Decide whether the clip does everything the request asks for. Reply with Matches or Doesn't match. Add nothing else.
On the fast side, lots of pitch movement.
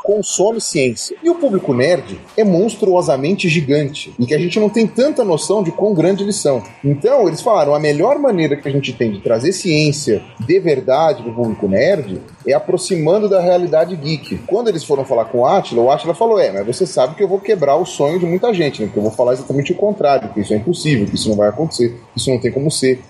Matches